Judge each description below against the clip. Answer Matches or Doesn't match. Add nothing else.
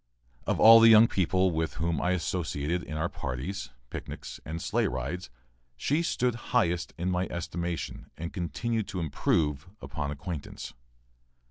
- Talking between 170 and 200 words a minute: Doesn't match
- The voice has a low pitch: Matches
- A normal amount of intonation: Matches